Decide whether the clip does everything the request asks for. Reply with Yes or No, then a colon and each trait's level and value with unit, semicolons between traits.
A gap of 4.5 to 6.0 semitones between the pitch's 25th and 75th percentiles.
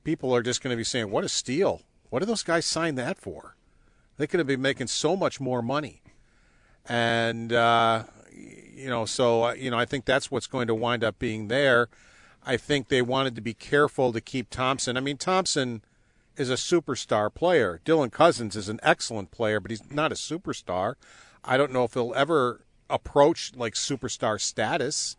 No: average, 3.3 semitones